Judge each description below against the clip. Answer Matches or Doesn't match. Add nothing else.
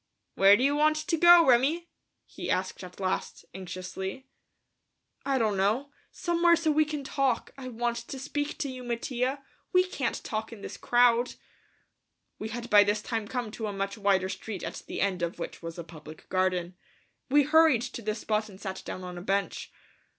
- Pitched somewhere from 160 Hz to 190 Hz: Doesn't match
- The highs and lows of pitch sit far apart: Matches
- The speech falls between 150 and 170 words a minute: Doesn't match